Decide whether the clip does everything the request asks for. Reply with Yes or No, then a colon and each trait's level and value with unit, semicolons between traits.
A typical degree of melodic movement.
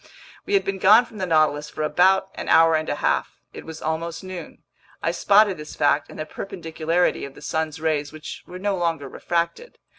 Yes: average, 3.5 semitones